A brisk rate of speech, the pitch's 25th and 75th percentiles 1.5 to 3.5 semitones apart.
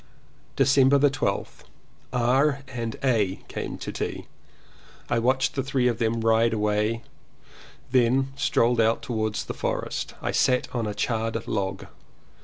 No: slow, 135 wpm; average, 2.8 semitones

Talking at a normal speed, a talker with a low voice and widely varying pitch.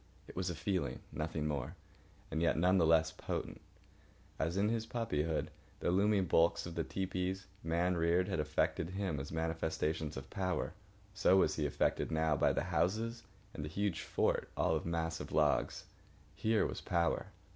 No: average, 170 wpm; very low, 85 Hz; average, 3.1 semitones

